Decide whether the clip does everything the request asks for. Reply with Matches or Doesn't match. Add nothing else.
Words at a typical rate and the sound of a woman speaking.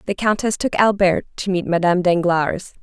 Matches